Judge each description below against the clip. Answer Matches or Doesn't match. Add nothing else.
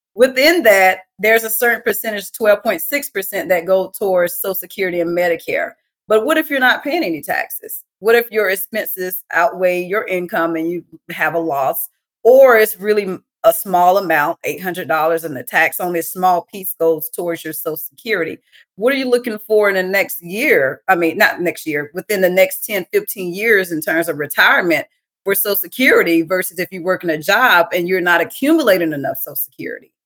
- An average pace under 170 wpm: Doesn't match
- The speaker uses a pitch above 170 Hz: Matches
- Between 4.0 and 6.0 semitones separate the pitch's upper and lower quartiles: Matches